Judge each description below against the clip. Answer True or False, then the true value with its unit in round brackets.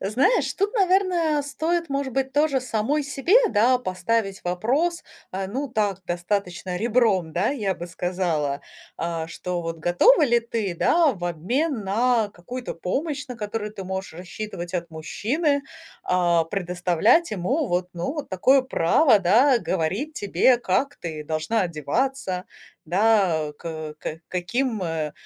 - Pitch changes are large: True (7.3 semitones)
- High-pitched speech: True (205 Hz)